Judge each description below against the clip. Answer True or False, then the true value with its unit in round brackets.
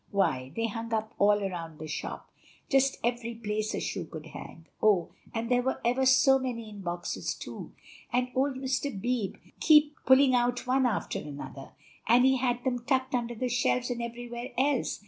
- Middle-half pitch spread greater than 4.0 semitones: False (3.7 semitones)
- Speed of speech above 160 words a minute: True (185 wpm)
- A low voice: False (240 Hz)